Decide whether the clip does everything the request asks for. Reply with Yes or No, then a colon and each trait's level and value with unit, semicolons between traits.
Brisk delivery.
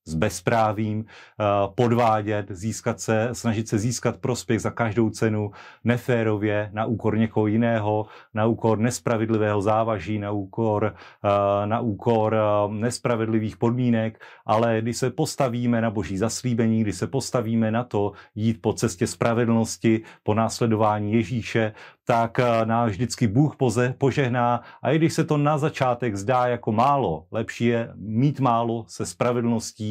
No: average, 135 wpm